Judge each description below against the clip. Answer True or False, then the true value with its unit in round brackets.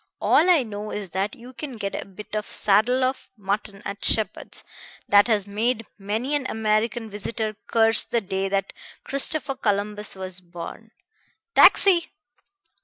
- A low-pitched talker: False (215 Hz)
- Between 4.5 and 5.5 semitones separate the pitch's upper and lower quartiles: False (3.2 semitones)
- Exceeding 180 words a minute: False (150 wpm)